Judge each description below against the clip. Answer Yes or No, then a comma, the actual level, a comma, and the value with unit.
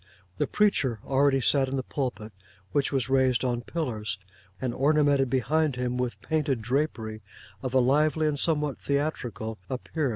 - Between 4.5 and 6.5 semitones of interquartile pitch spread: No, average, 3.0 semitones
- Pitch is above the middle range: No, low, 135 Hz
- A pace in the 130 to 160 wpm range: Yes, average, 155 wpm